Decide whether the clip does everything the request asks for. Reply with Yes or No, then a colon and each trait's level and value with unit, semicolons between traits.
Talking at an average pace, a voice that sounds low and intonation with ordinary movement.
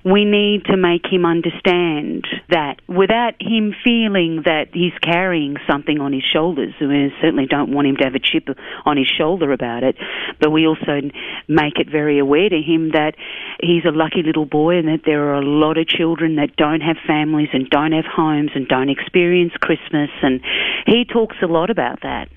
No: average, 195 wpm; medium, 160 Hz; average, 3.1 semitones